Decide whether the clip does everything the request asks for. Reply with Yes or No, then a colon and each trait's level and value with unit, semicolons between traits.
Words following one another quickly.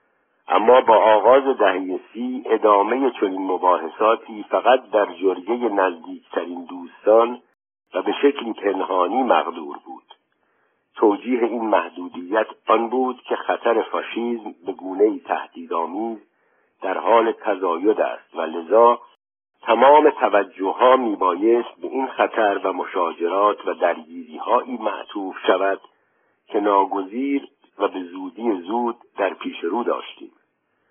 No: average, 115 wpm